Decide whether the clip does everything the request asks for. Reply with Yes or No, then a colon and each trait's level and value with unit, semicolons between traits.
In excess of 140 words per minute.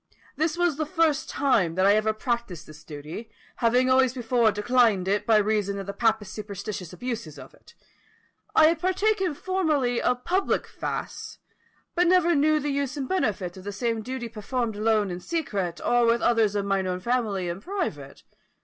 Yes: average, 180 wpm